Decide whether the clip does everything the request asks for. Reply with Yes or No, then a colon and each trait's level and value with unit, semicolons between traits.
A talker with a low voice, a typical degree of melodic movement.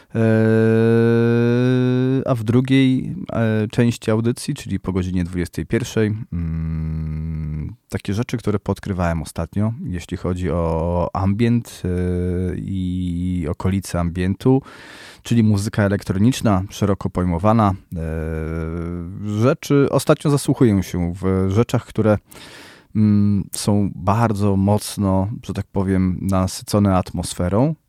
Yes: low, 100 Hz; average, 4.3 semitones